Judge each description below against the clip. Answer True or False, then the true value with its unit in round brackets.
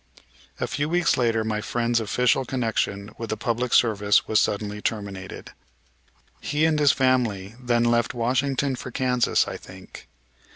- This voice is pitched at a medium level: False (120 Hz)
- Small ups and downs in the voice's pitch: False (3.2 semitones)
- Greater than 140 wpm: True (150 wpm)